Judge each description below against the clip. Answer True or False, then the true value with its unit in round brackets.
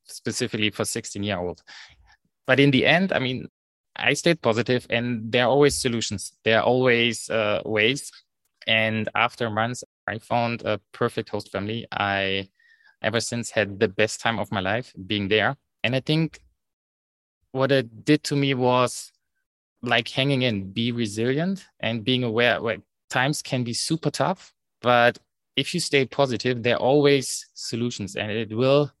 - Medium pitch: False (120 Hz)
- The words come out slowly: False (160 wpm)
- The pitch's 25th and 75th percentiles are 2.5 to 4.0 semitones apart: True (3.3 semitones)